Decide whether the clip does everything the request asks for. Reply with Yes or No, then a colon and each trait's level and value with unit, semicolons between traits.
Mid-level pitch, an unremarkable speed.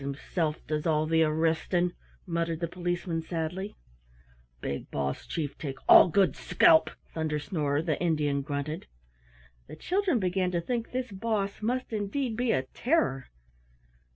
Yes: medium, 170 Hz; average, 145 wpm